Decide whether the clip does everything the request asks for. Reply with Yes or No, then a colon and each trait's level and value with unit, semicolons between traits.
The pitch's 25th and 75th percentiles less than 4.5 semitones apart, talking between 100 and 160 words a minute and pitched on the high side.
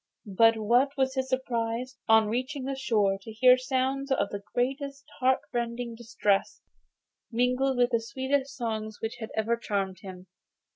Yes: average, 3.0 semitones; average, 150 wpm; high, 240 Hz